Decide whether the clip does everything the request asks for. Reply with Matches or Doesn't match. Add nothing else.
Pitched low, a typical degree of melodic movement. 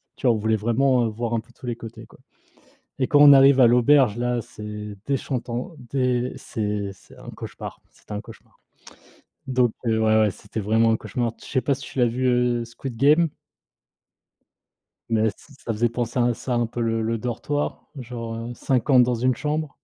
Doesn't match